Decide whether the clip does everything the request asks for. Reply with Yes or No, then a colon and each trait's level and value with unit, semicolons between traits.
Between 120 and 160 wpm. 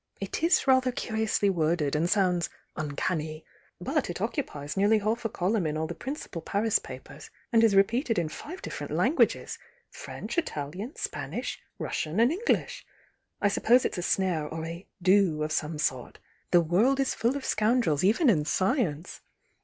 No: average, 170 wpm